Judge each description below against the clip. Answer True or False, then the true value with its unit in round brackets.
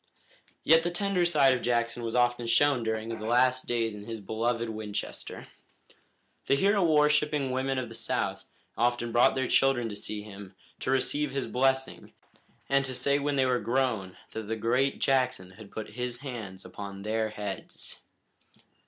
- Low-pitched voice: True (120 Hz)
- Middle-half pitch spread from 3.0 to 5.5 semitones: True (3.3 semitones)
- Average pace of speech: True (170 wpm)